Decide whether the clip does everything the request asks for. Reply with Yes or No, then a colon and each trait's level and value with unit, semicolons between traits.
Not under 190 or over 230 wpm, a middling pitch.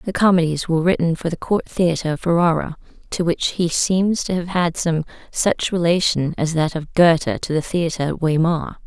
Yes: average, 195 wpm; medium, 170 Hz